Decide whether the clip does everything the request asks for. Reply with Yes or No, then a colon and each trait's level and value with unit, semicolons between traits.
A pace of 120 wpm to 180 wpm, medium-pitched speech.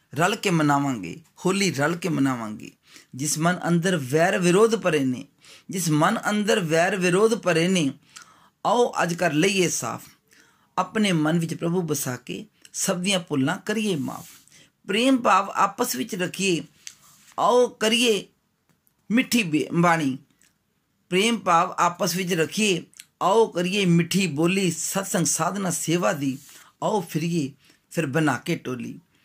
Yes: average, 135 wpm; medium, 175 Hz